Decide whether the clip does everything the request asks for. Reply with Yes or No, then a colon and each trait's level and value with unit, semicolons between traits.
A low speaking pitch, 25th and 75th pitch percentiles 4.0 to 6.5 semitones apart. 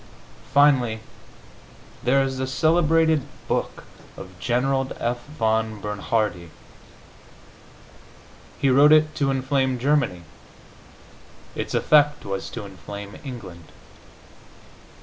Yes: low, 130 Hz; average, 5.3 semitones